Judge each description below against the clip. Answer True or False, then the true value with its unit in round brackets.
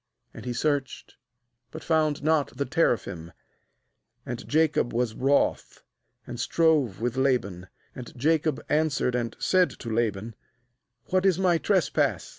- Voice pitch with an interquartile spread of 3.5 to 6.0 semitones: True (5.0 semitones)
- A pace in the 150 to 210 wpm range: False (135 wpm)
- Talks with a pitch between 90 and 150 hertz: True (135 Hz)